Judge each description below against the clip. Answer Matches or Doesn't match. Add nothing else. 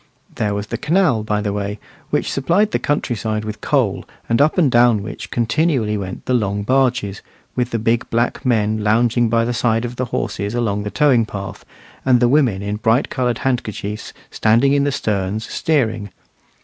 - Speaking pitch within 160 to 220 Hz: Doesn't match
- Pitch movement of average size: Matches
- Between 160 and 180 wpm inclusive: Doesn't match